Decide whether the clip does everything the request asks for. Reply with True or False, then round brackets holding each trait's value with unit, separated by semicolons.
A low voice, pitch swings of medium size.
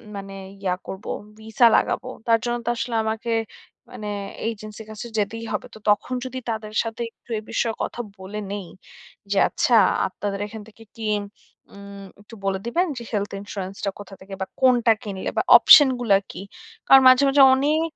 False (220 Hz; 3.0 semitones)